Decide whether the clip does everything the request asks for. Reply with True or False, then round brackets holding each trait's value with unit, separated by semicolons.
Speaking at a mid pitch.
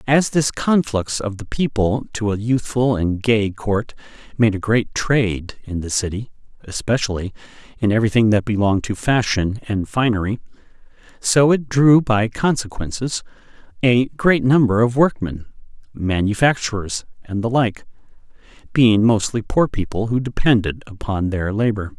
False (115 Hz)